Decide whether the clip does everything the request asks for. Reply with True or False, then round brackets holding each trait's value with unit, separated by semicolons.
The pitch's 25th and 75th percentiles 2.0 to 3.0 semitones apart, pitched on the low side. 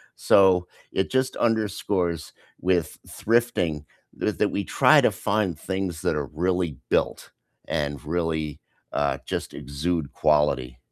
False (4.4 semitones; 85 Hz)